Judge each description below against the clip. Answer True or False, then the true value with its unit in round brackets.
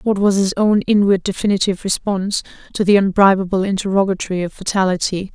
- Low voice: False (195 Hz)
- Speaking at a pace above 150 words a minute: False (145 wpm)